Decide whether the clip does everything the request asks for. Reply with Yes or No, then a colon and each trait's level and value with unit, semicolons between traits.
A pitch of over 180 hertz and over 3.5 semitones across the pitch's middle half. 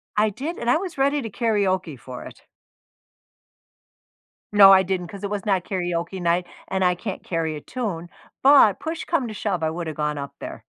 Yes: high, 190 Hz; average, 4.8 semitones